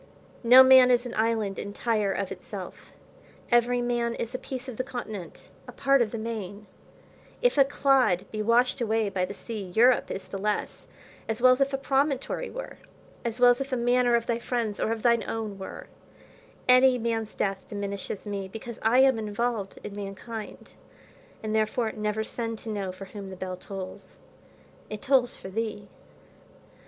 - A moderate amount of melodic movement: Yes, average, 3.2 semitones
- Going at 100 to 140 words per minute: No, average, 185 wpm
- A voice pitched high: Yes, high, 225 Hz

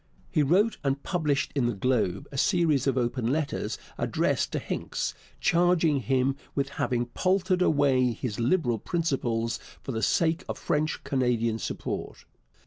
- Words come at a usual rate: Yes, average, 145 wpm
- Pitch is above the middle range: No, low, 135 Hz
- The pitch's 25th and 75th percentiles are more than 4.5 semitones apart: Yes, average, 4.9 semitones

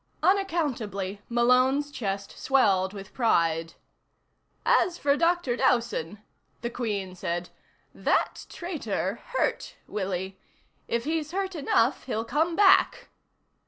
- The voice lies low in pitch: No, high, 235 Hz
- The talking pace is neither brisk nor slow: No, slow, 105 wpm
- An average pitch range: No, wide, 7.9 semitones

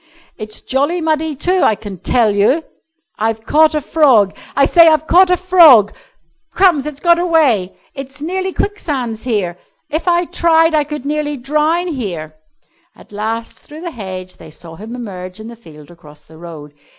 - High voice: Yes, very high, 270 Hz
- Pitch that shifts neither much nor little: No, wide, 7.8 semitones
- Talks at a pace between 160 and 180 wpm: Yes, average, 175 wpm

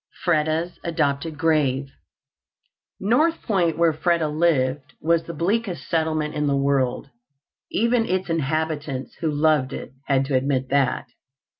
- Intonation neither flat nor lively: Yes, average, 3.3 semitones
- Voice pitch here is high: No, medium, 155 Hz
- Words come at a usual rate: No, slow, 130 wpm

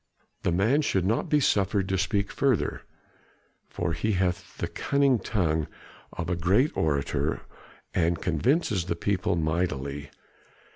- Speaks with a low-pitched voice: Yes, very low, 90 Hz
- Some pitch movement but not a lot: Yes, average, 4.4 semitones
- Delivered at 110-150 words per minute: Yes, slow, 135 wpm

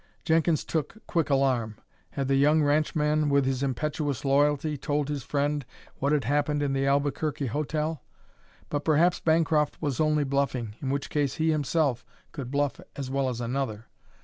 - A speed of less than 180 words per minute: Yes, average, 165 wpm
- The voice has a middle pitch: Yes, medium, 145 Hz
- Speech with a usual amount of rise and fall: No, narrow, 1.9 semitones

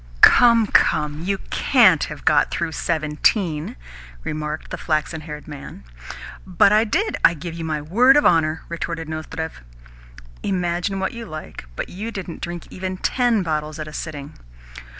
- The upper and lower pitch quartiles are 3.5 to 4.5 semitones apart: Yes, average, 4.0 semitones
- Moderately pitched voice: Yes, medium, 165 Hz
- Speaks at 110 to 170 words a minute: Yes, average, 150 wpm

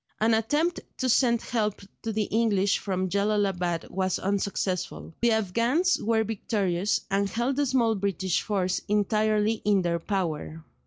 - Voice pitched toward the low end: No, high, 210 Hz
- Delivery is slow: No, average, 145 wpm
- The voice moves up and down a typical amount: Yes, average, 3.1 semitones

